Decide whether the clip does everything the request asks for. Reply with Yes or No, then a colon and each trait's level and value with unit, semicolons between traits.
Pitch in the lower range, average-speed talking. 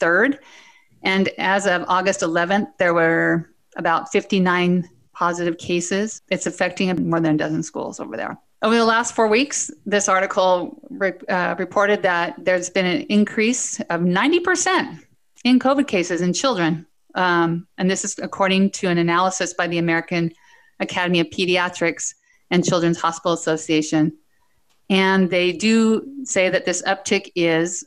No: medium, 185 Hz; average, 150 wpm